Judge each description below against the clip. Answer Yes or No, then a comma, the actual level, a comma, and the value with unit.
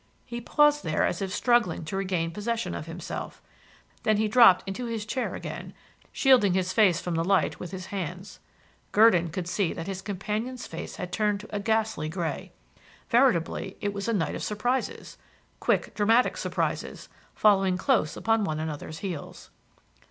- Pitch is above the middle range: Yes, high, 200 Hz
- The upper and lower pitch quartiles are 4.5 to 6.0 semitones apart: No, average, 4.1 semitones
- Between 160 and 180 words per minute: Yes, average, 165 wpm